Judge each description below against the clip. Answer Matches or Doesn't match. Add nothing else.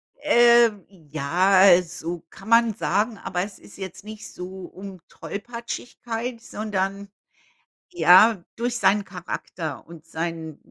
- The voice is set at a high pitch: Matches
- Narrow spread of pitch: Doesn't match